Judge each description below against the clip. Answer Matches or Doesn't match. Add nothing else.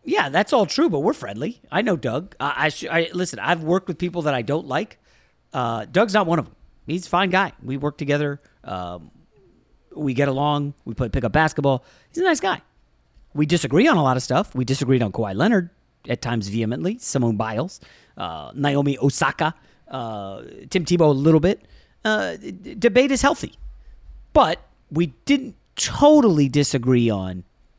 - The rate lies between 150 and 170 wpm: Doesn't match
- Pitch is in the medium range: Matches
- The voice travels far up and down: Matches